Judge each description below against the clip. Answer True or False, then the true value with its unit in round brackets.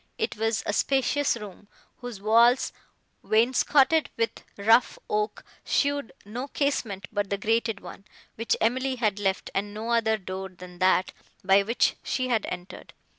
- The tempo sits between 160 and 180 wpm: False (150 wpm)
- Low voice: False (220 Hz)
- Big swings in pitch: False (3.6 semitones)